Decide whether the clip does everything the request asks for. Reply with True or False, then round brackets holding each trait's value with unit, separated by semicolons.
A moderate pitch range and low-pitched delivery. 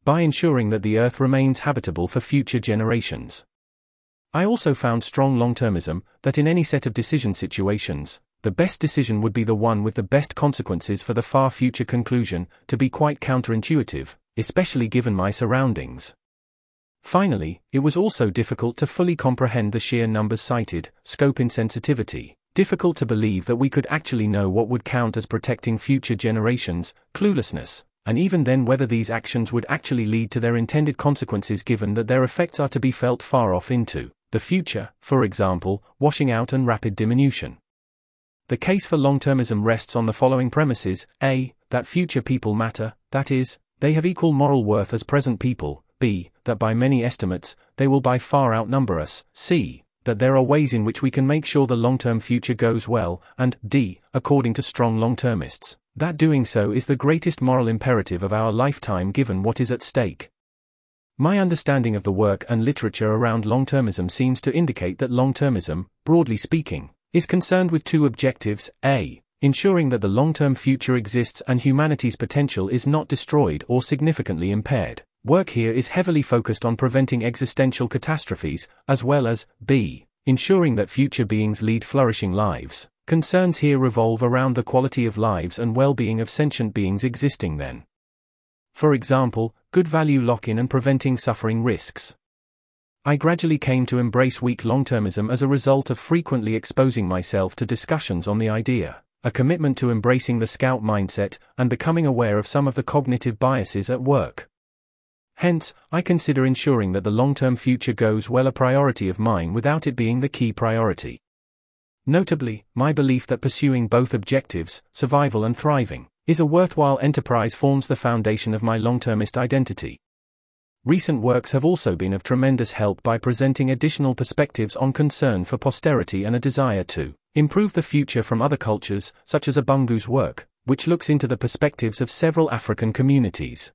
True (3.8 semitones; 125 Hz)